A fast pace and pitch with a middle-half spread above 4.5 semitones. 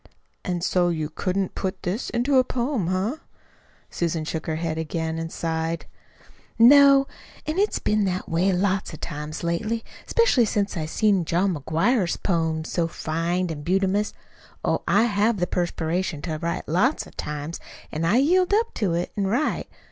No: average, 170 wpm; average, 4.9 semitones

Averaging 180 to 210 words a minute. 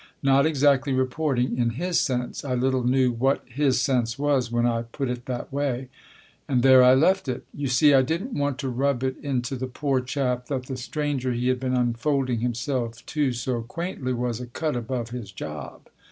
Yes: average, 195 wpm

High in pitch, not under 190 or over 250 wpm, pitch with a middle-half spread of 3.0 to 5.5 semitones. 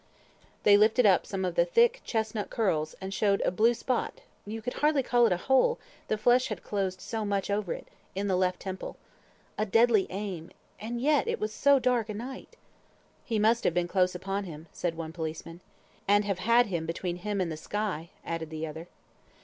Yes: high, 205 Hz; fast, 205 wpm; average, 4.2 semitones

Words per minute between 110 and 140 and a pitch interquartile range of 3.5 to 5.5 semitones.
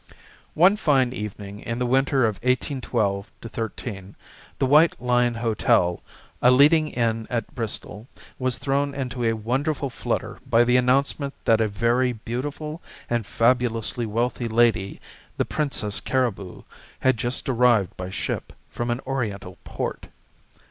No: slow, 135 wpm; average, 2.8 semitones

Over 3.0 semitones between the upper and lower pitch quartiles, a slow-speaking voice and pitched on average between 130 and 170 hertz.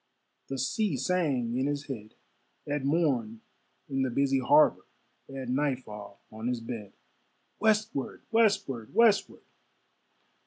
Yes: average, 3.9 semitones; slow, 115 wpm; low, 135 Hz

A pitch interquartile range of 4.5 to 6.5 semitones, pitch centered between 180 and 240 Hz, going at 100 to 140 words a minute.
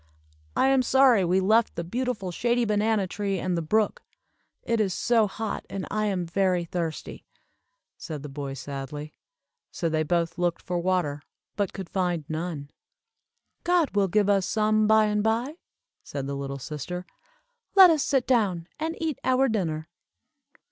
No: average, 4.9 semitones; high, 190 Hz; average, 160 wpm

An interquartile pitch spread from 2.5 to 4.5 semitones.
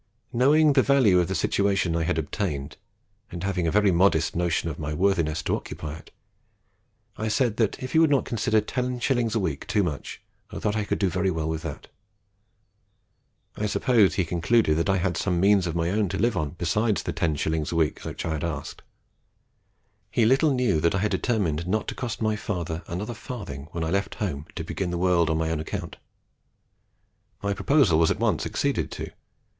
No: average, 5.0 semitones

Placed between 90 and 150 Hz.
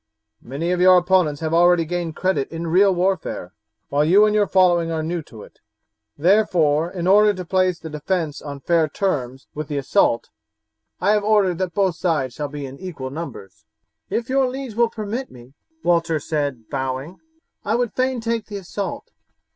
No: medium, 175 Hz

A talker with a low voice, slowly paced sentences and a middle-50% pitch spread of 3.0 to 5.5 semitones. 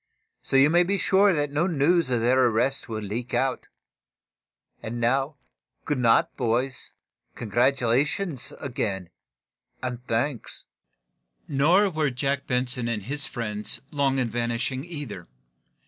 Yes: low, 130 Hz; slow, 130 wpm; average, 3.7 semitones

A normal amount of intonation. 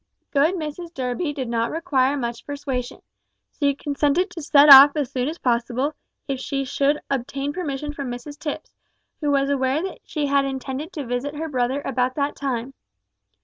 No: narrow, 2.3 semitones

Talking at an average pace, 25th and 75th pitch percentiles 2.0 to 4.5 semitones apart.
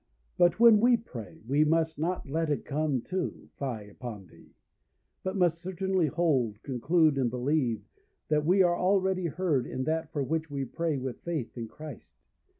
No: average, 170 wpm; average, 4.9 semitones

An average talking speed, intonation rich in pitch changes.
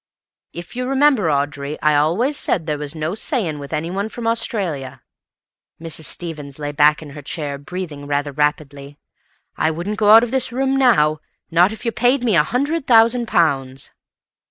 Yes: average, 175 wpm; wide, 7.6 semitones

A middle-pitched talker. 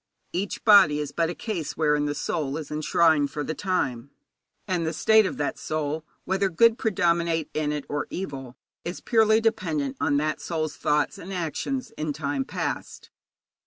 Yes: medium, 160 Hz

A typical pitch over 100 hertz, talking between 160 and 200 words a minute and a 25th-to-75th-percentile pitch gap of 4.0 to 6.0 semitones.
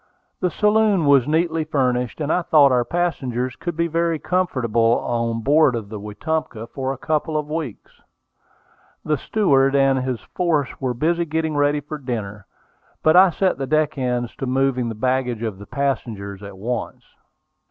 Yes: low, 135 Hz; average, 170 wpm; average, 4.7 semitones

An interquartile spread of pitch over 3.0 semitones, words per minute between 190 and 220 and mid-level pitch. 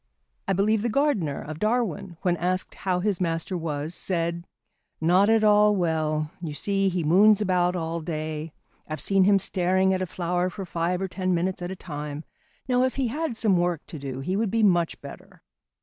Yes: average, 3.4 semitones; average, 195 wpm; medium, 180 Hz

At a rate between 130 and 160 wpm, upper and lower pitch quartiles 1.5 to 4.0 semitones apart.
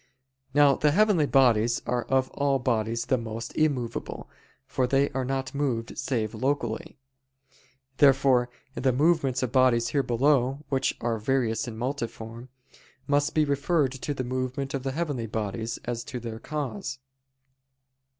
Yes: average, 145 wpm; average, 3.1 semitones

